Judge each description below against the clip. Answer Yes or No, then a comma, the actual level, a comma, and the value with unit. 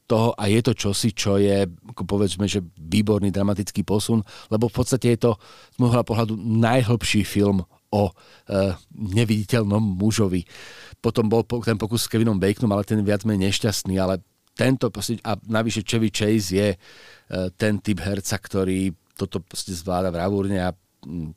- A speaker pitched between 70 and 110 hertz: Yes, low, 105 Hz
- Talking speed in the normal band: Yes, average, 155 wpm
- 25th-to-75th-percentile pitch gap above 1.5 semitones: Yes, narrow, 2.6 semitones